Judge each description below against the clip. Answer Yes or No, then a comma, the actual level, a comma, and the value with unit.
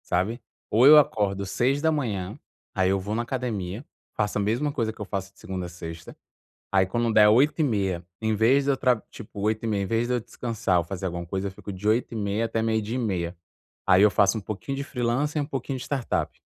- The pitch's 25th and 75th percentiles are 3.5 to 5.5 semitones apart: Yes, average, 4.2 semitones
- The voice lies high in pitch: No, low, 110 Hz